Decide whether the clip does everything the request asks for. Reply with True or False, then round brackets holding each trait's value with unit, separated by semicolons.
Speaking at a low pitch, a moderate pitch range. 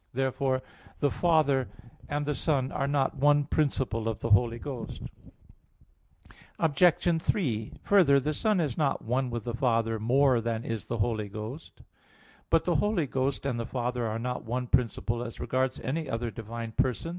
True (130 Hz; 3.7 semitones)